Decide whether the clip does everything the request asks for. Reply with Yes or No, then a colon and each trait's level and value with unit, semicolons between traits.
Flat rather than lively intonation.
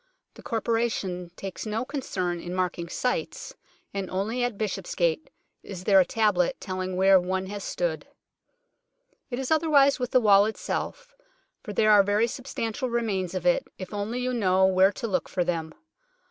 No: average, 4.1 semitones